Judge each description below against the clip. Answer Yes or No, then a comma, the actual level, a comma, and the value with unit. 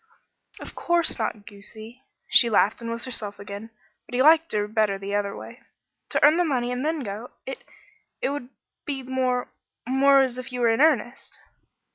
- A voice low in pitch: No, high, 245 Hz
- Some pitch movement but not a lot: Yes, average, 3.9 semitones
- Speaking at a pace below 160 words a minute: No, average, 185 wpm